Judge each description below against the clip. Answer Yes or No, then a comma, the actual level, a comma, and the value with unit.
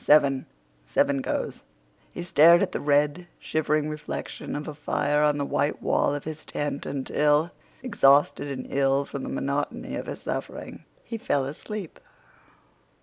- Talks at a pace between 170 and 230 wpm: No, average, 150 wpm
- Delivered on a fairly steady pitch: Yes, narrow, 1.5 semitones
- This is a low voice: No, medium, 145 Hz